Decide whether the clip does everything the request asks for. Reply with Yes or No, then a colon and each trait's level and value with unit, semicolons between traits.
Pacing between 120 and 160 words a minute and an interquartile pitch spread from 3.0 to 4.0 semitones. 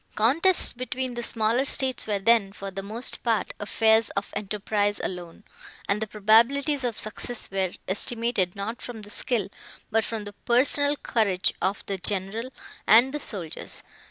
Yes: average, 155 wpm; average, 3.4 semitones